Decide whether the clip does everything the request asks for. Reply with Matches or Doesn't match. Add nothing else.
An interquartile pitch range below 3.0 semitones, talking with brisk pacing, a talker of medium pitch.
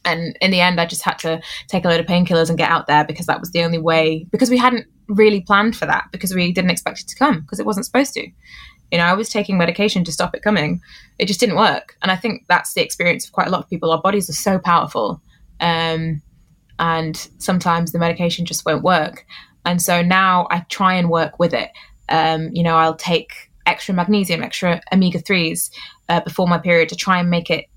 Matches